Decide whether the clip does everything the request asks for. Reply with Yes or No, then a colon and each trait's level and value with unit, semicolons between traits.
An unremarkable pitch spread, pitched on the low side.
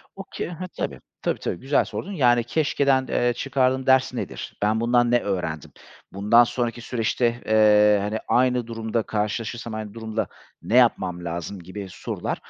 Yes: average, 3.1 semitones; low, 115 Hz